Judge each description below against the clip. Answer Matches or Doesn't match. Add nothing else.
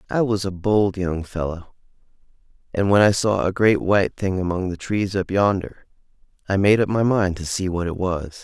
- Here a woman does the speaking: Doesn't match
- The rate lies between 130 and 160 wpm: Doesn't match